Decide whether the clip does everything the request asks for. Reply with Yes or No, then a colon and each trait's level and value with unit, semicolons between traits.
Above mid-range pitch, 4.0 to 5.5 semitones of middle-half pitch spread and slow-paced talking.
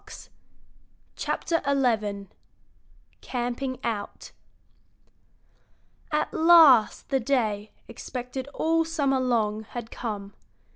Yes: very high, 250 Hz; average, 4.4 semitones; slow, 75 wpm